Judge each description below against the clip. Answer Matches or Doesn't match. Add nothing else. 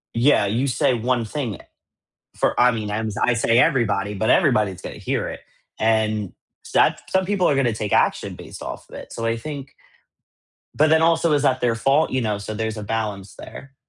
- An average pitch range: Matches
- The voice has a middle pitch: Doesn't match